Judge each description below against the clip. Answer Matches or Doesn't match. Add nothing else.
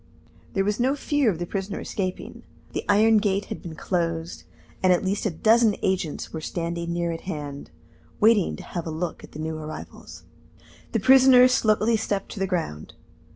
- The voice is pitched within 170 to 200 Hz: Matches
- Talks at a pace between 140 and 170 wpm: Doesn't match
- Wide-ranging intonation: Doesn't match